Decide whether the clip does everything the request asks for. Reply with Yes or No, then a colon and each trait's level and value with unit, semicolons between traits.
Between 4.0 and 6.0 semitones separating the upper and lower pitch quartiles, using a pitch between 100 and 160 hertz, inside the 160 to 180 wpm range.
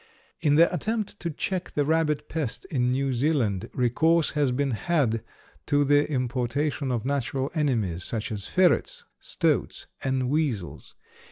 No: average, 4.3 semitones; medium, 140 Hz; average, 150 wpm